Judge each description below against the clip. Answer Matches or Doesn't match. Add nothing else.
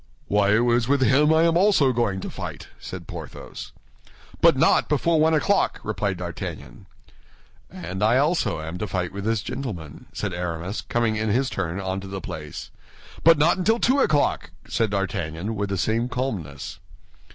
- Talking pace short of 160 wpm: Doesn't match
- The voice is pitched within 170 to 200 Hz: Doesn't match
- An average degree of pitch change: Doesn't match